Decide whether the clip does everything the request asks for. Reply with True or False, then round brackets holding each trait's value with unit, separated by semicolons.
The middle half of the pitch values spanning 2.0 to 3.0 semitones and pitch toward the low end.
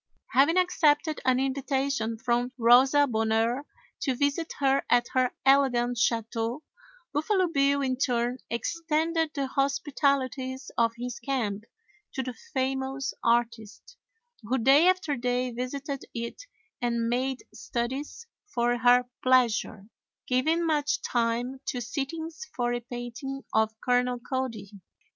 False (2.7 semitones; 255 Hz)